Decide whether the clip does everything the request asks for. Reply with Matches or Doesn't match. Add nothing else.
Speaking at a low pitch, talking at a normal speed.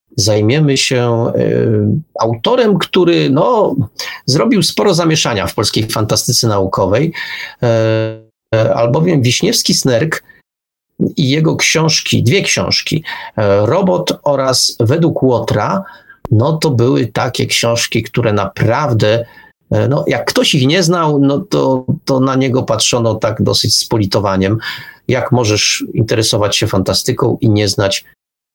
Matches